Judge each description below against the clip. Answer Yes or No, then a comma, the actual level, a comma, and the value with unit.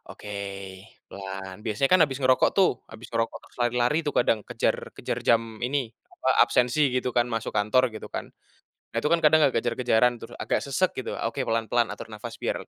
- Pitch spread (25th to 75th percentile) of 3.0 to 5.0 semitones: No, narrow, 2.5 semitones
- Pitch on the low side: Yes, low, 120 Hz